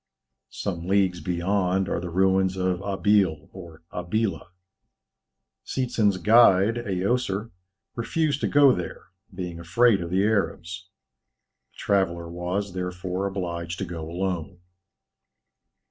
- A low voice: Yes, very low, 95 Hz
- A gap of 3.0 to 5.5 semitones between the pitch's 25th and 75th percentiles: No, narrow, 2.4 semitones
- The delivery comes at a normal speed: No, slow, 115 wpm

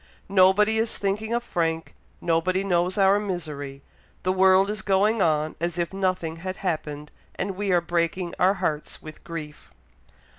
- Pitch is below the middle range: No, medium, 185 Hz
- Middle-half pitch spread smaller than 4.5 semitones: Yes, average, 3.1 semitones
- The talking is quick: No, average, 155 wpm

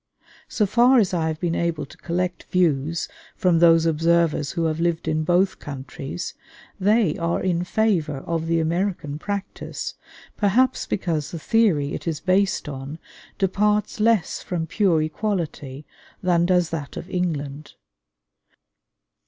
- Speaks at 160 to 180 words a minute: No, average, 140 wpm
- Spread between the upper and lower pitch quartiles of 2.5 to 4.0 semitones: Yes, average, 3.4 semitones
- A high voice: No, medium, 170 Hz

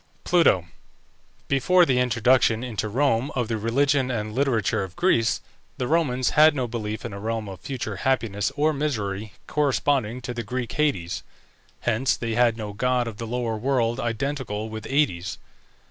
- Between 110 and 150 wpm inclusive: No, average, 160 wpm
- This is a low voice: Yes, low, 120 Hz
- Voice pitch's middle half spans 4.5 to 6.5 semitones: No, average, 3.7 semitones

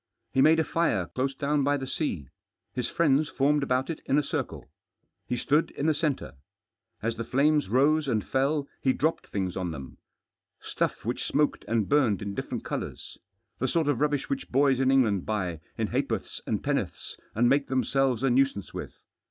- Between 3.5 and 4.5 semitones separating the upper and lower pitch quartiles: Yes, average, 4.1 semitones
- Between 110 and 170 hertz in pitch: Yes, low, 135 Hz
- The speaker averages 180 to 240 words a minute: Yes, average, 185 wpm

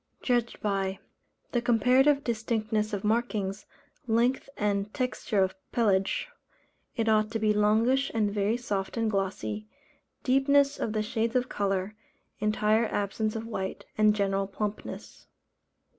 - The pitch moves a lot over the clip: No, average, 2.8 semitones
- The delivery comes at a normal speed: No, slow, 130 wpm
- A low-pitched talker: No, high, 215 Hz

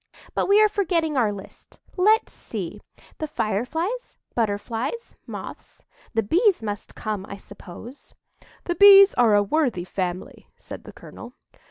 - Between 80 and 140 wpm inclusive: Yes, slow, 135 wpm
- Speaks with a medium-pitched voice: No, very high, 250 Hz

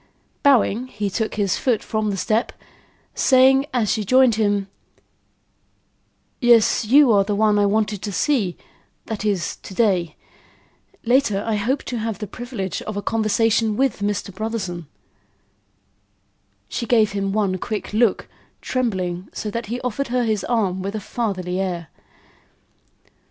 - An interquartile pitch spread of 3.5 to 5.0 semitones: No, average, 3.0 semitones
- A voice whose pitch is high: Yes, high, 215 Hz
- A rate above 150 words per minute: No, average, 145 wpm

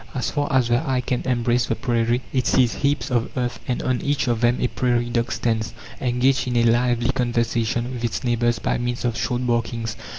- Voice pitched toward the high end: No, low, 120 Hz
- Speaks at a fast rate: Yes, fast, 210 wpm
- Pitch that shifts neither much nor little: No, narrow, 1.2 semitones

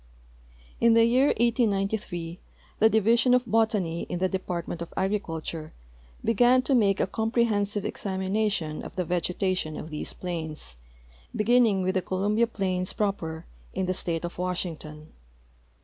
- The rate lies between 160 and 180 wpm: No, slow, 135 wpm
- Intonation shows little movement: No, average, 4.2 semitones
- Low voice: No, high, 190 Hz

